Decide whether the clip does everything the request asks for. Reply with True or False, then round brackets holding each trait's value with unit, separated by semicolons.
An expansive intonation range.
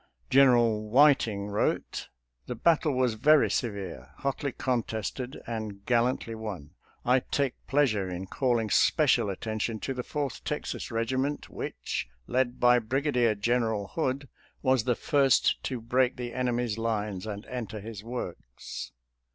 False (3.5 semitones)